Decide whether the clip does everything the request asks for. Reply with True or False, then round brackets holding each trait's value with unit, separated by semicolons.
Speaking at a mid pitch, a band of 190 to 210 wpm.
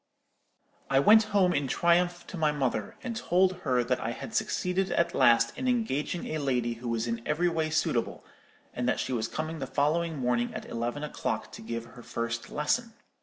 True (150 Hz; 195 wpm)